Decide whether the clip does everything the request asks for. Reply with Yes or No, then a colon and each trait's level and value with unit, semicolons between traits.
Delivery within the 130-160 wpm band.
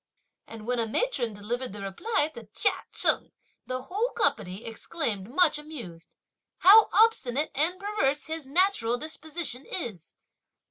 Yes: slow, 135 wpm